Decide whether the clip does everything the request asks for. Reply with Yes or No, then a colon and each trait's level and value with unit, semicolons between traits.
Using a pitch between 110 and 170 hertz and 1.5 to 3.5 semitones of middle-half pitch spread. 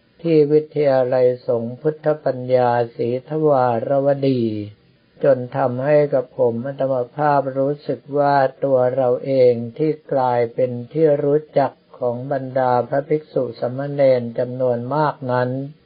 Yes: low, 135 Hz; average, 2.7 semitones